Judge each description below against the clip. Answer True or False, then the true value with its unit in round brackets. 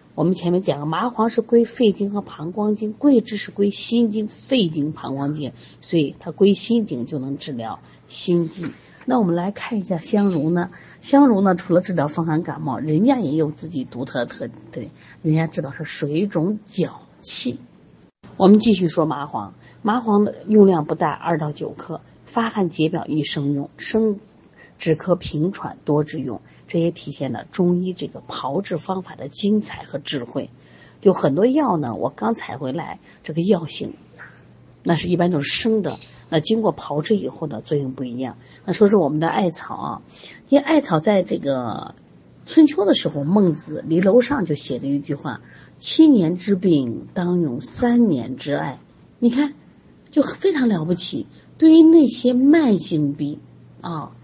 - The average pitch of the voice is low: False (175 Hz)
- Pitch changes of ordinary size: False (6.0 semitones)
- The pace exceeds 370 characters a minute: False (250 characters per minute)